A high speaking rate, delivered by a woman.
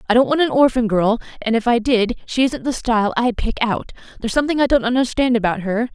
Yes: fast, 240 wpm; female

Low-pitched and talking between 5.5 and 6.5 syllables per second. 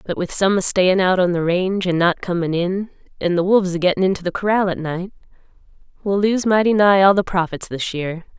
No: medium, 185 Hz; 5.8 syllables/s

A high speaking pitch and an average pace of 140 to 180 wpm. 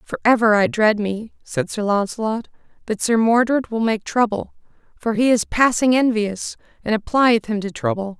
Yes: high, 225 Hz; average, 175 wpm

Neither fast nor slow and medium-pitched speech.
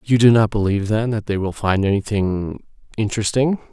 No: average, 160 wpm; low, 105 Hz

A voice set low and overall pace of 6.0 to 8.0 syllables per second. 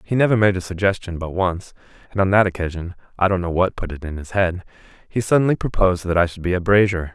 No: very low, 95 Hz; 5.5 syllables/s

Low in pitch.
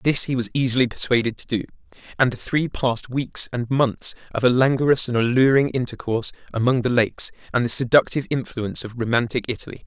Yes: low, 125 Hz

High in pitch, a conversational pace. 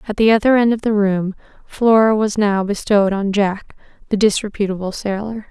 Yes: high, 205 Hz; average, 175 wpm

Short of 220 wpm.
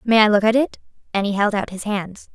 No: fast, 280 wpm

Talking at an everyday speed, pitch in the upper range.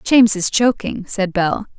Yes: average, 170 wpm; high, 205 Hz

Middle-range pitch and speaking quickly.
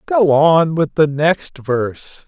No: medium, 155 Hz; average, 160 wpm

